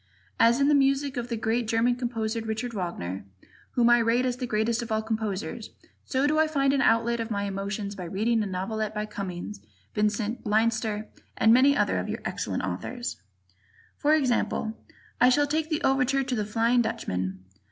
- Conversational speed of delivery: Yes, average, 185 wpm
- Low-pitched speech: No, high, 230 Hz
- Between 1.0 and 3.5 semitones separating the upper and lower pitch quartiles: Yes, average, 3.0 semitones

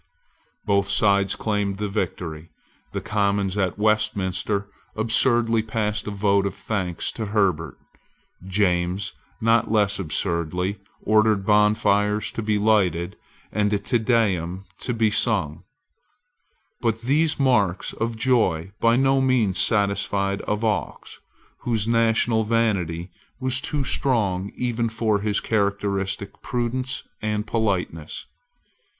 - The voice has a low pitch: Yes, low, 105 Hz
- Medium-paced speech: No, slow, 115 wpm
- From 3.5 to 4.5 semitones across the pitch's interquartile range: No, narrow, 2.5 semitones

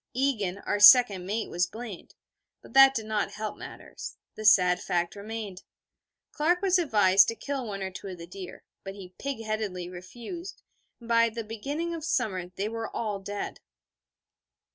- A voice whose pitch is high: Yes, high, 215 Hz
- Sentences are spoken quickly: No, average, 170 wpm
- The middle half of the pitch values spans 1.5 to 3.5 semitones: No, average, 4.1 semitones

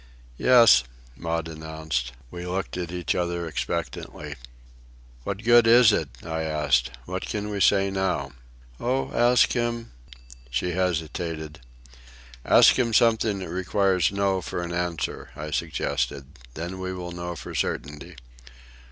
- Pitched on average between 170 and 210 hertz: No, very low, 90 Hz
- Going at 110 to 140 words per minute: Yes, slow, 135 wpm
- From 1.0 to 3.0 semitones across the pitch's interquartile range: No, average, 4.0 semitones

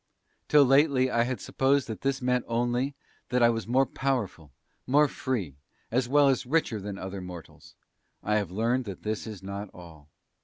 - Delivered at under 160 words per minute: No, average, 180 wpm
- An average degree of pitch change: Yes, average, 4.8 semitones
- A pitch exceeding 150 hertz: No, low, 120 Hz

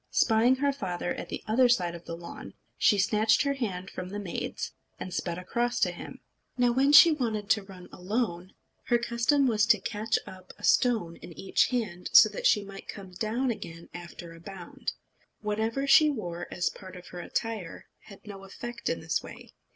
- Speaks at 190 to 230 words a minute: Yes, average, 195 wpm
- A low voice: No, high, 210 Hz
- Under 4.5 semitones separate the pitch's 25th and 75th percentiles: No, average, 4.8 semitones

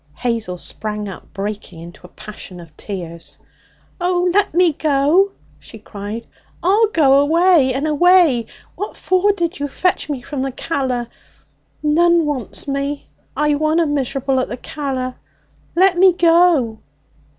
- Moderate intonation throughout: No, wide, 6.4 semitones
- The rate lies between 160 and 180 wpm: No, average, 140 wpm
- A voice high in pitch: Yes, very high, 285 Hz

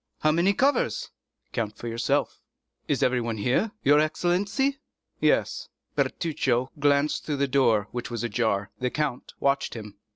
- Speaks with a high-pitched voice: No, low, 135 Hz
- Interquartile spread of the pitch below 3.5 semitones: No, average, 4.8 semitones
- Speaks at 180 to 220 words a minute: No, average, 140 wpm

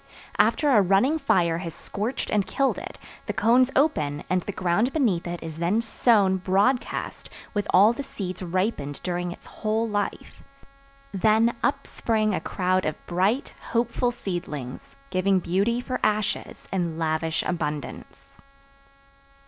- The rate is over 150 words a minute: No, average, 140 wpm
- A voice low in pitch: No, high, 195 Hz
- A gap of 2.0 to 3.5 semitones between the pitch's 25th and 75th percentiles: No, average, 4.7 semitones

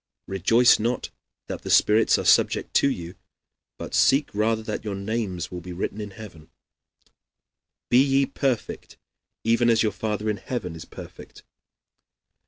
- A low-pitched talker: Yes, low, 110 Hz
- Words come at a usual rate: Yes, average, 145 wpm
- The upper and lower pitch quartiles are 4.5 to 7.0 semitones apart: No, average, 3.6 semitones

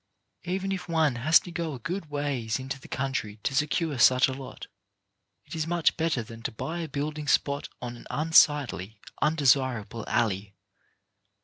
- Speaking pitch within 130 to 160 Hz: Yes, medium, 140 Hz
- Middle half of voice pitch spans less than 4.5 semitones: No, average, 4.9 semitones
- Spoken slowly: No, average, 170 wpm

